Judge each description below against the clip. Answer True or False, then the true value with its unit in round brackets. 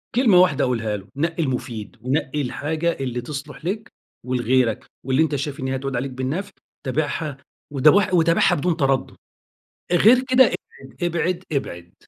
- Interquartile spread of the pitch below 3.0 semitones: False (4.7 semitones)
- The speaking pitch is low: False (145 Hz)